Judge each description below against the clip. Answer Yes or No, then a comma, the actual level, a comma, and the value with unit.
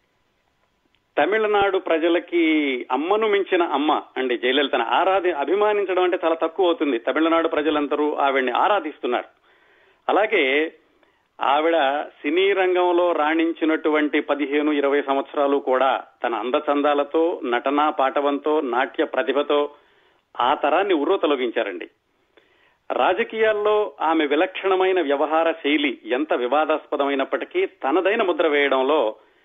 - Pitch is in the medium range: Yes, medium, 155 Hz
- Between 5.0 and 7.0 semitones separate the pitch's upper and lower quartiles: No, average, 4.0 semitones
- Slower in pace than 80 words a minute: No, average, 95 wpm